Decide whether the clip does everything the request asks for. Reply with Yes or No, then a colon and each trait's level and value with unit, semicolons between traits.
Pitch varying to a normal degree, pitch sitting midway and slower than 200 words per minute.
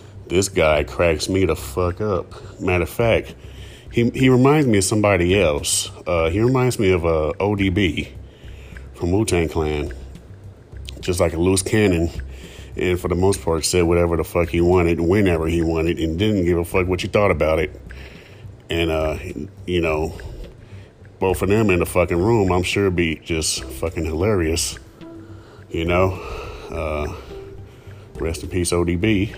No: average, 3.3 semitones; very low, 90 Hz; average, 165 wpm